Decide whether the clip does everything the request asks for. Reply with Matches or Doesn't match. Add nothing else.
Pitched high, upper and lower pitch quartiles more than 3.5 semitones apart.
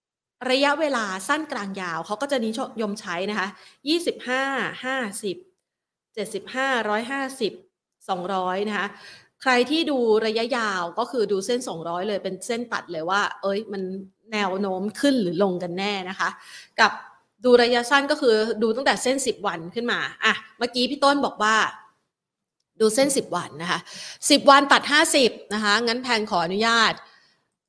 Matches